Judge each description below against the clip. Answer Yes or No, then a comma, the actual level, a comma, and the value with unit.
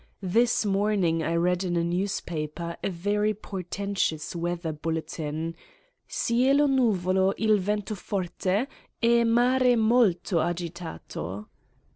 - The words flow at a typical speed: No, slow, 105 wpm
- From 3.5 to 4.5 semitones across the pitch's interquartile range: Yes, average, 4.1 semitones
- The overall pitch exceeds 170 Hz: Yes, medium, 185 Hz